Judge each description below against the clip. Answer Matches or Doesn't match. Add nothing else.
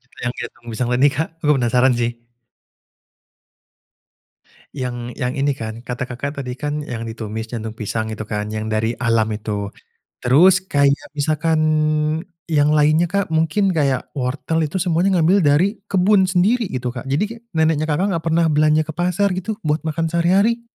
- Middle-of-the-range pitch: Matches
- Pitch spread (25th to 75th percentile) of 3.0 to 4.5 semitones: Doesn't match